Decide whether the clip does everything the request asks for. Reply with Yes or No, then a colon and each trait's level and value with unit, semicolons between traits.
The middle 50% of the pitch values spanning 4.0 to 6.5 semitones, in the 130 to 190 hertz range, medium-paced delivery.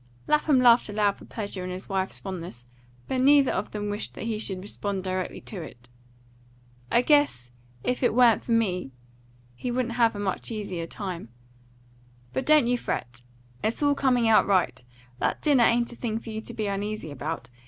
No: average, 4.6 semitones; high, 210 Hz; average, 185 wpm